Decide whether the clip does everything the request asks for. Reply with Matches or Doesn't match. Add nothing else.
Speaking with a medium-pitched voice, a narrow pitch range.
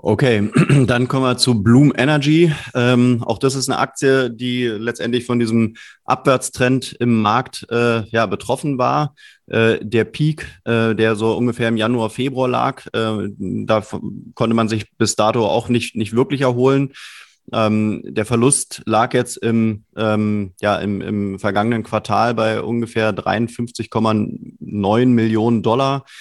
Doesn't match